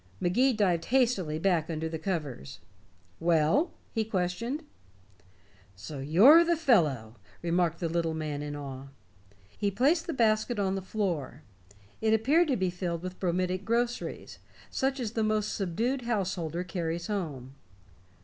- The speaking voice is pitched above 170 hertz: Yes, medium, 185 Hz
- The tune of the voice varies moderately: No, wide, 5.9 semitones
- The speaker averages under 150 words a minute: Yes, average, 140 wpm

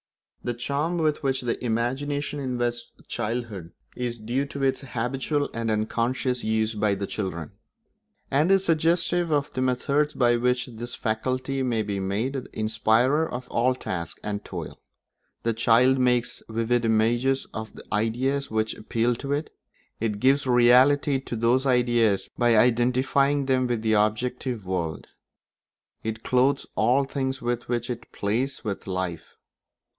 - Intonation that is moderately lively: Yes, average, 3.3 semitones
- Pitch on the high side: No, low, 120 Hz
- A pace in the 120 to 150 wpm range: Yes, average, 145 wpm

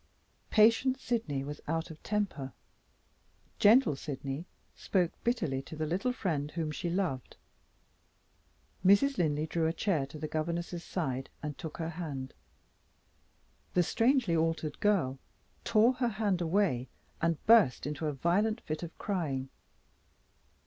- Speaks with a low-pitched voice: No, medium, 165 Hz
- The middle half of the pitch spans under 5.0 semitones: No, wide, 5.6 semitones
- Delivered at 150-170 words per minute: No, slow, 135 wpm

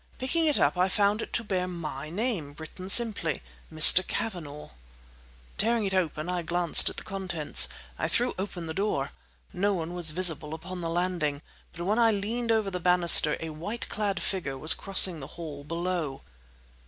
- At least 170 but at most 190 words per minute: Yes, average, 175 wpm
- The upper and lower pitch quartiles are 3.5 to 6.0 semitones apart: Yes, average, 4.0 semitones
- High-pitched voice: No, medium, 180 Hz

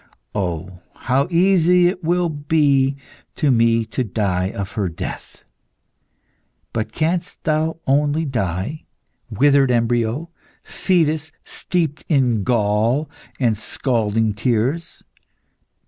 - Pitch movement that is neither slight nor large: No, wide, 6.3 semitones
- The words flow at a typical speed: No, slow, 100 wpm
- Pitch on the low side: Yes, low, 130 Hz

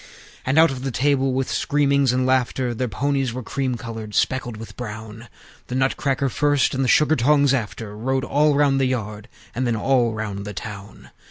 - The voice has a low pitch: Yes, low, 130 Hz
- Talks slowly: No, average, 190 wpm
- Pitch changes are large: No, average, 3.5 semitones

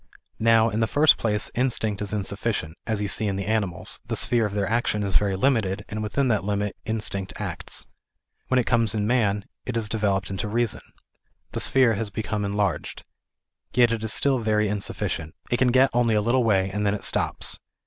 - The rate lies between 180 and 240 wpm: Yes, average, 200 wpm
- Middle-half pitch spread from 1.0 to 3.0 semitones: Yes, narrow, 2.5 semitones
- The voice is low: Yes, low, 105 Hz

